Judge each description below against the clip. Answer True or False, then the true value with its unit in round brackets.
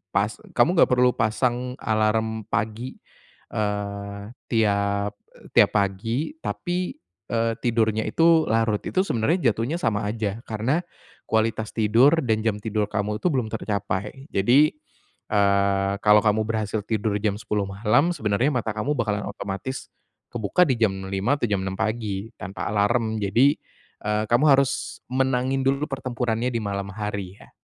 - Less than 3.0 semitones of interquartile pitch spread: False (3.3 semitones)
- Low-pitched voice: True (110 Hz)